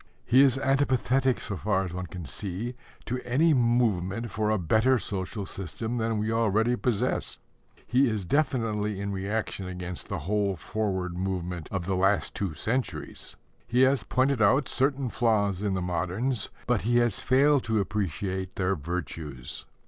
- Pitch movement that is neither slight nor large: Yes, average, 4.7 semitones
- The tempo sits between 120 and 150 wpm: No, average, 160 wpm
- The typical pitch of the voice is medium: No, low, 105 Hz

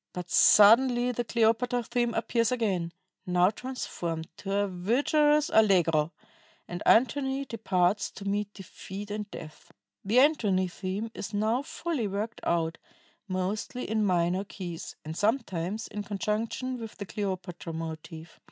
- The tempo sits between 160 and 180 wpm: No, slow, 135 wpm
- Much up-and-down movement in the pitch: No, average, 4.5 semitones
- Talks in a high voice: Yes, high, 205 Hz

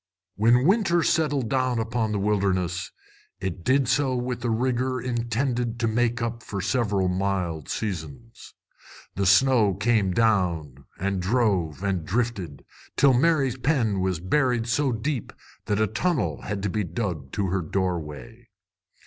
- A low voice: Yes, low, 110 Hz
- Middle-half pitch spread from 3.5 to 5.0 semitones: Yes, average, 4.6 semitones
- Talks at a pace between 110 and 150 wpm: Yes, average, 145 wpm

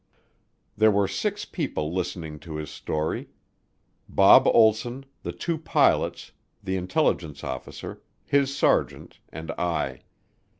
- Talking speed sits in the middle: No, slow, 115 wpm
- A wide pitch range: Yes, wide, 6.1 semitones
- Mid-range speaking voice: No, very low, 90 Hz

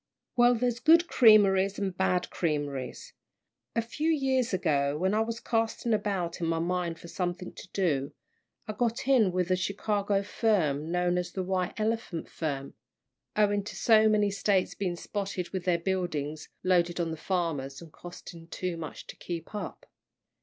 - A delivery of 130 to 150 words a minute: No, average, 165 wpm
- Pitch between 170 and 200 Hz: Yes, medium, 185 Hz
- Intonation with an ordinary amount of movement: Yes, average, 4.0 semitones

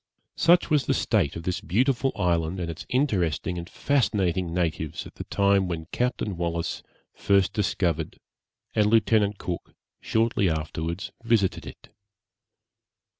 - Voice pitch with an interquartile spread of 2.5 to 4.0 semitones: No, average, 4.6 semitones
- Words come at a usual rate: No, slow, 130 wpm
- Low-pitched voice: Yes, very low, 95 Hz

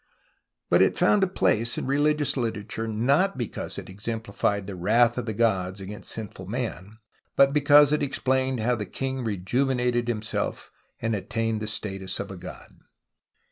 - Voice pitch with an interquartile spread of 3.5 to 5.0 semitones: Yes, average, 4.2 semitones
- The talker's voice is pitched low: Yes, low, 115 Hz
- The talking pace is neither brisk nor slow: Yes, average, 160 wpm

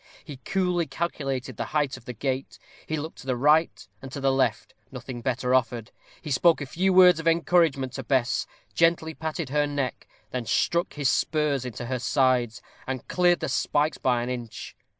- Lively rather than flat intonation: No, average, 4.0 semitones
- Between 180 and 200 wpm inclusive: Yes, average, 190 wpm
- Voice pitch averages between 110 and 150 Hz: Yes, low, 135 Hz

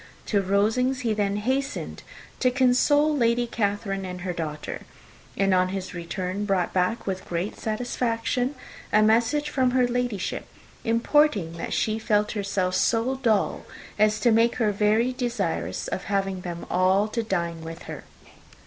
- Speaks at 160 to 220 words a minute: No, average, 150 wpm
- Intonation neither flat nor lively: Yes, average, 4.3 semitones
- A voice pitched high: Yes, high, 215 Hz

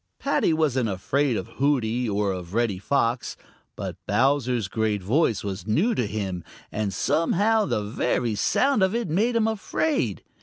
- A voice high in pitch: No, low, 120 Hz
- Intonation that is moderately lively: No, wide, 8.2 semitones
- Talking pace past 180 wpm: No, average, 155 wpm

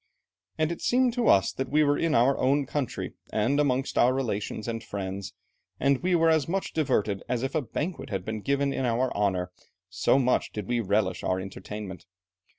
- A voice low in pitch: Yes, low, 125 Hz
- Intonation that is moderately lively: No, wide, 5.8 semitones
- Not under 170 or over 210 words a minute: Yes, average, 195 wpm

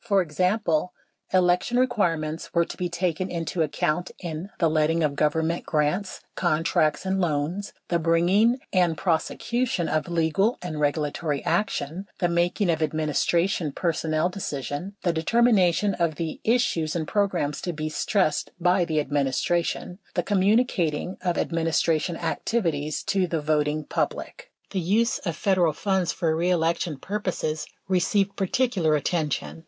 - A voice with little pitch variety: No, average, 3.4 semitones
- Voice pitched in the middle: Yes, medium, 170 Hz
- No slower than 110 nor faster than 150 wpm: Yes, average, 140 wpm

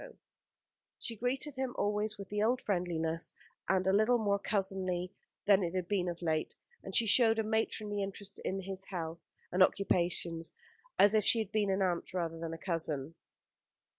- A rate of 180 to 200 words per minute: No, average, 170 wpm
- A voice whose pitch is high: Yes, high, 195 Hz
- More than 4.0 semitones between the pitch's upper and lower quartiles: No, average, 3.3 semitones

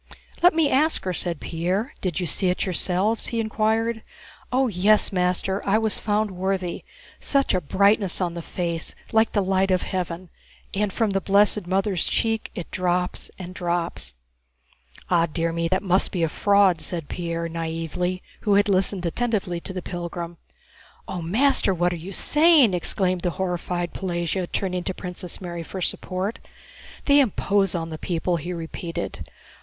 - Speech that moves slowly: No, average, 165 wpm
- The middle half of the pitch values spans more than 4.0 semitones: No, average, 2.9 semitones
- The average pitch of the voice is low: No, medium, 185 Hz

